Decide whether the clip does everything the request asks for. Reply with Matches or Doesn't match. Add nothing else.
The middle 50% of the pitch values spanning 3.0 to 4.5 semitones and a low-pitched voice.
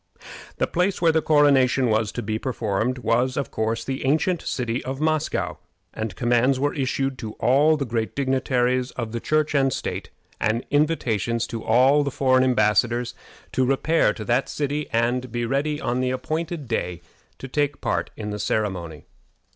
Matches